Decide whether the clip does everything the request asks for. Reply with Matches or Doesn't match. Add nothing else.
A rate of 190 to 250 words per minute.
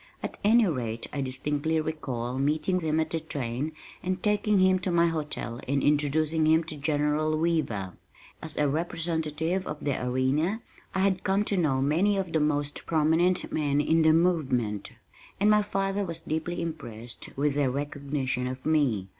Doesn't match